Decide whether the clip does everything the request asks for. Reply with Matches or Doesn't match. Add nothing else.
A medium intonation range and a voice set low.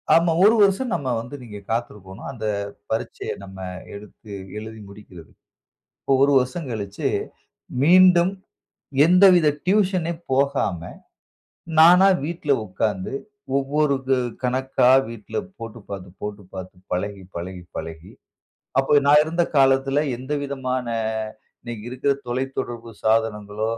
Doesn't match